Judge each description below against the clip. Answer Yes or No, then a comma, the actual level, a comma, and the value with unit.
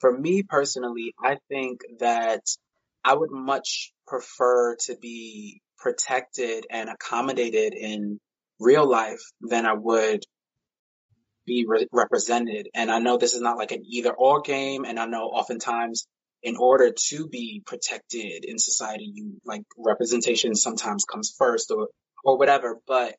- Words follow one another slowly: No, average, 145 wpm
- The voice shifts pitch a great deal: No, average, 3.5 semitones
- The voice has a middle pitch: No, low, 120 Hz